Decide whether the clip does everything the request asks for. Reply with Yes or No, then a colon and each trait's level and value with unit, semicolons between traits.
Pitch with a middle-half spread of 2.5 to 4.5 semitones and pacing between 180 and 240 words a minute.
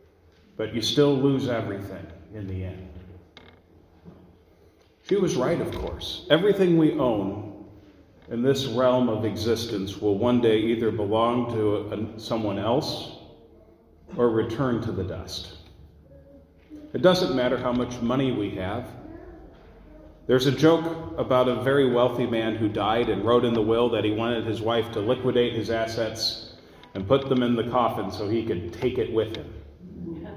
No: average, 3.8 semitones; average, 160 wpm